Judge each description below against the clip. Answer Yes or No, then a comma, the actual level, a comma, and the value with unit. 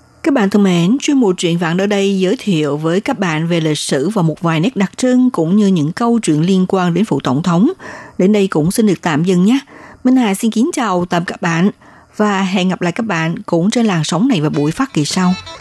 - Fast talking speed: Yes, fast, 260 wpm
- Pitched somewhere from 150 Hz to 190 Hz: Yes, medium, 185 Hz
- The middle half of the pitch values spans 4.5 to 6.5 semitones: No, average, 4.0 semitones